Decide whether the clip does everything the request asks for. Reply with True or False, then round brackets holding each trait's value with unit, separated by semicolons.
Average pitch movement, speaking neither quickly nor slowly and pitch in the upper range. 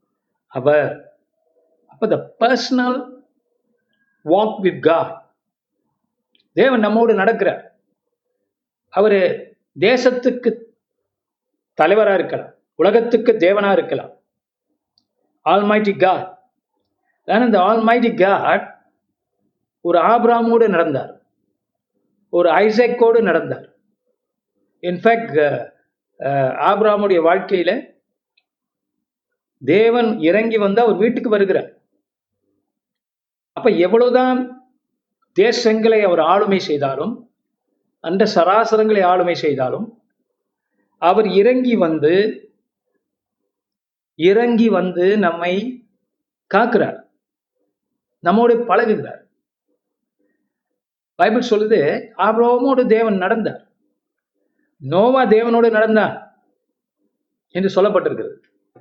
False (4.7 semitones; 60 wpm; 225 Hz)